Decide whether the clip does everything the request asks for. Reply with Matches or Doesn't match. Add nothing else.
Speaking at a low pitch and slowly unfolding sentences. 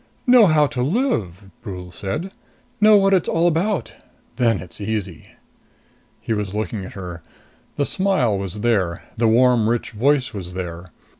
Doesn't match